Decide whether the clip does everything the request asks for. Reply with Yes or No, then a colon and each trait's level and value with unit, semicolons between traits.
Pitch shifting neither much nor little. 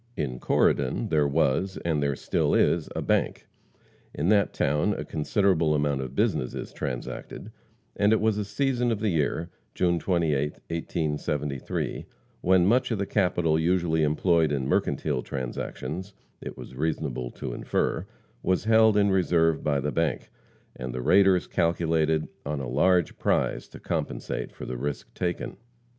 Yes: average, 4.6 semitones